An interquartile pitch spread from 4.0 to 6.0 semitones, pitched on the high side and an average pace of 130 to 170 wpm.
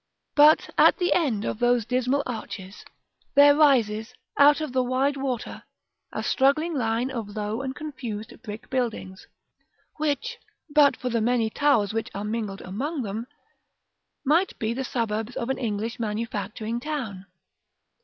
Yes: average, 4.4 semitones; high, 245 Hz; average, 145 wpm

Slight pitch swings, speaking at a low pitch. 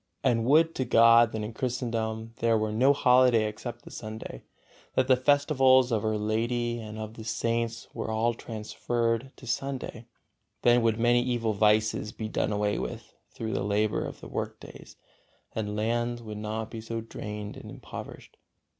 Yes: narrow, 1.9 semitones; low, 115 Hz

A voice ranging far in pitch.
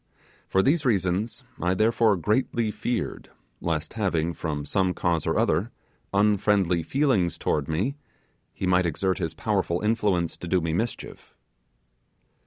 No: average, 4.2 semitones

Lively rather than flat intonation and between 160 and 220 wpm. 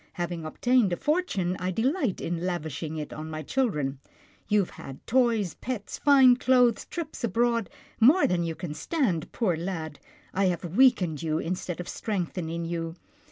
Yes: wide, 6.6 semitones; average, 165 wpm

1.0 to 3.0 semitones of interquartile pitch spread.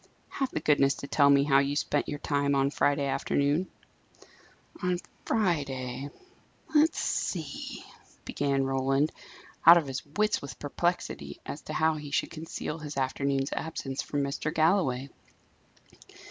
Yes: narrow, 2.5 semitones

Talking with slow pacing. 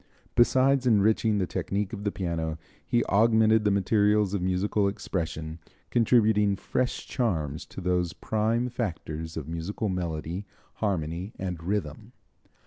Yes: slow, 130 wpm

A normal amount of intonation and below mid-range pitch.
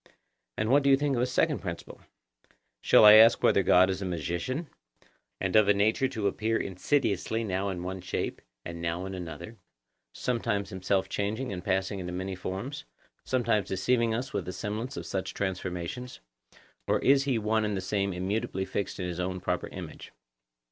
Yes: average, 3.7 semitones; low, 100 Hz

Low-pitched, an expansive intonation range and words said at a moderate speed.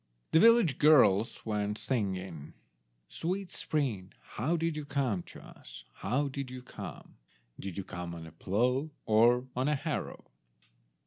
Yes: low, 125 Hz; wide, 6.9 semitones; average, 145 wpm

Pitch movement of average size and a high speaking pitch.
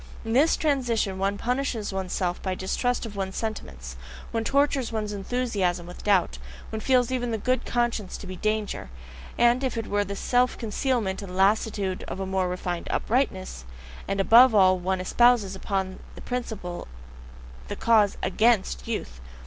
Yes: average, 4.2 semitones; high, 205 Hz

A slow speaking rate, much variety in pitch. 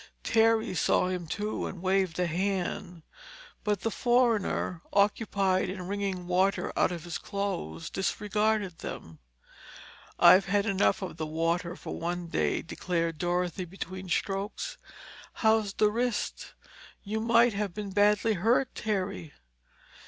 No: slow, 130 wpm; average, 3.0 semitones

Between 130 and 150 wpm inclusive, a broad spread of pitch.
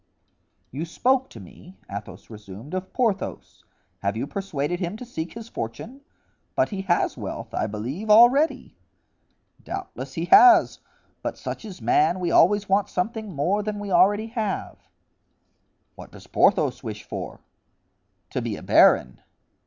Yes: average, 145 wpm; wide, 7.4 semitones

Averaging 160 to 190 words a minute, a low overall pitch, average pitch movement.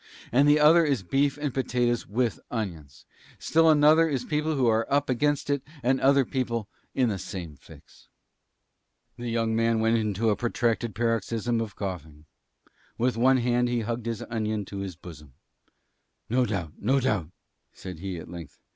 Yes: average, 180 wpm; low, 115 Hz; average, 4.5 semitones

